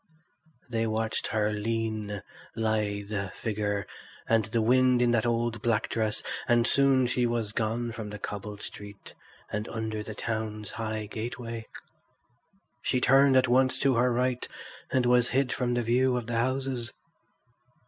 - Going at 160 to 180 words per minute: No, average, 150 wpm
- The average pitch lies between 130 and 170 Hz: No, low, 115 Hz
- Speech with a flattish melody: Yes, narrow, 2.3 semitones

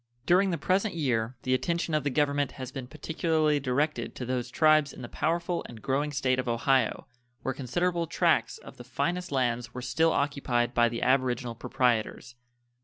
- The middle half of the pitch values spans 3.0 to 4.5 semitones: Yes, average, 3.9 semitones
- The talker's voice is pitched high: No, low, 135 Hz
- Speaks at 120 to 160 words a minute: No, average, 180 wpm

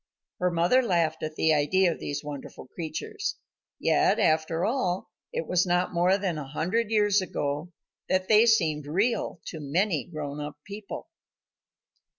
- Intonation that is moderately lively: Yes, average, 4.4 semitones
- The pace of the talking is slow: No, average, 155 wpm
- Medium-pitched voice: Yes, medium, 175 Hz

